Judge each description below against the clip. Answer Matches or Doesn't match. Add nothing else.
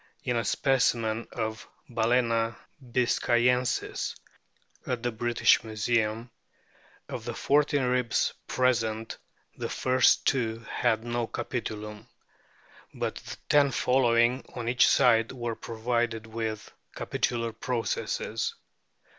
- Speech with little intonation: Matches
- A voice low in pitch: Matches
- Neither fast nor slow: Doesn't match